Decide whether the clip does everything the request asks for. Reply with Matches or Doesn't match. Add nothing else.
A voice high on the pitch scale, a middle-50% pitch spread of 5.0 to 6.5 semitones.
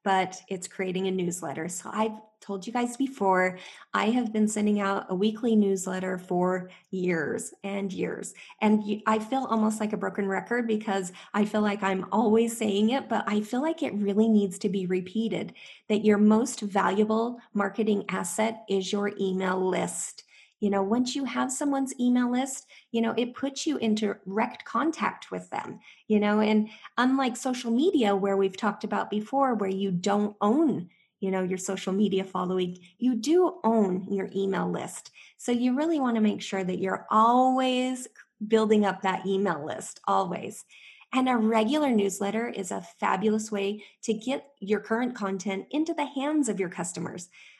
Doesn't match